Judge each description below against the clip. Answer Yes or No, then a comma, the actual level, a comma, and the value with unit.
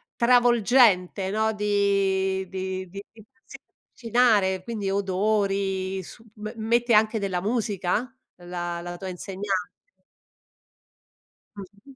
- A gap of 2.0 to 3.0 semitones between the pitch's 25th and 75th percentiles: Yes, narrow, 2.6 semitones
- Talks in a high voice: Yes, high, 200 Hz